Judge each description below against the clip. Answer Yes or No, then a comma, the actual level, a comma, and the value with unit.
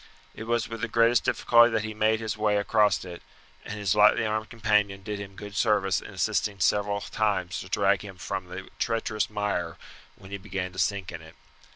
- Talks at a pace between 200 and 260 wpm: Yes, fast, 205 wpm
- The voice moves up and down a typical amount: No, narrow, 2.1 semitones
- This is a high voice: No, low, 105 Hz